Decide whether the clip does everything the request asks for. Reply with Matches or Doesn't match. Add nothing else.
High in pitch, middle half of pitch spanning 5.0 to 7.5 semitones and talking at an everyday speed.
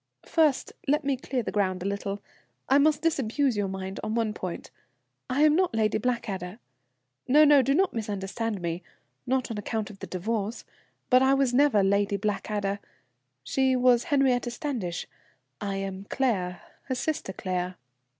Matches